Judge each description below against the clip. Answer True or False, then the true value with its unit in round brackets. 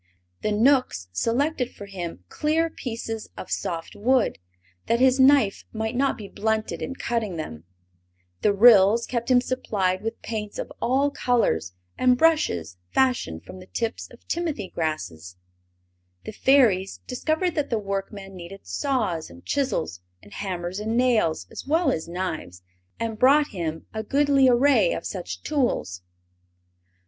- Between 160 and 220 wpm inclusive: False (145 wpm)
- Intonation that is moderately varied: False (6.2 semitones)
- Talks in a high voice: True (220 Hz)